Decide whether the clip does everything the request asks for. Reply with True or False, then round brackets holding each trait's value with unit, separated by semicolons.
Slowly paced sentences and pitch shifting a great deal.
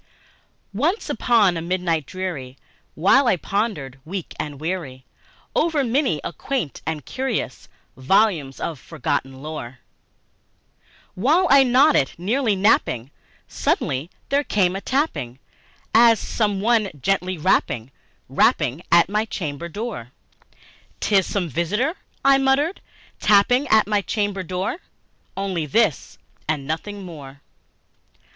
True (120 wpm; 7.0 semitones)